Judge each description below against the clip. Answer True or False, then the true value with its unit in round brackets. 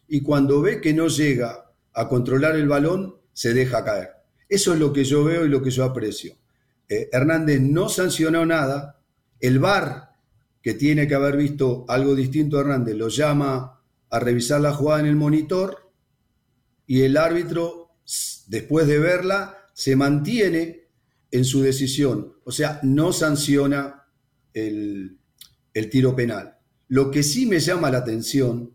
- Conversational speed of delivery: True (155 wpm)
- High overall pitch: False (140 Hz)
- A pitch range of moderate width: True (3.4 semitones)